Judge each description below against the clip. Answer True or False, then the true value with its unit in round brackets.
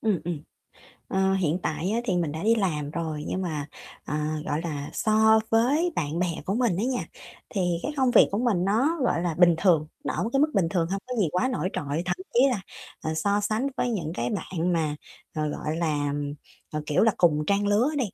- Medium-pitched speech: True (180 Hz)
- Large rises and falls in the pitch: True (5.8 semitones)